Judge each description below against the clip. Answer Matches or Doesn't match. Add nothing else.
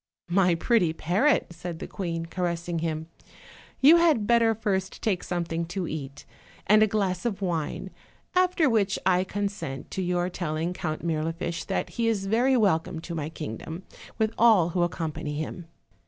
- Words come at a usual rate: Matches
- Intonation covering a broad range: Doesn't match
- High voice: Doesn't match